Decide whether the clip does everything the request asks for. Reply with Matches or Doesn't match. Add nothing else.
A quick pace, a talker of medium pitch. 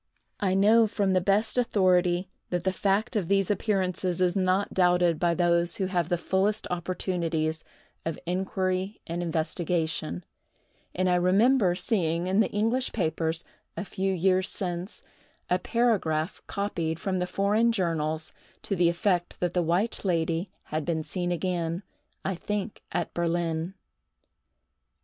Doesn't match